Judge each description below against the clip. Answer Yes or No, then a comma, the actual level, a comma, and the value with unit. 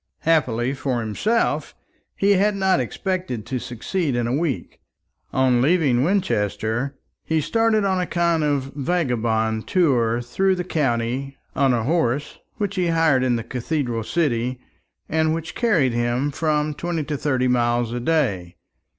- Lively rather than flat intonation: Yes, wide, 5.8 semitones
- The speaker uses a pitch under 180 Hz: Yes, medium, 140 Hz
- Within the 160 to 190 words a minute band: No, average, 150 wpm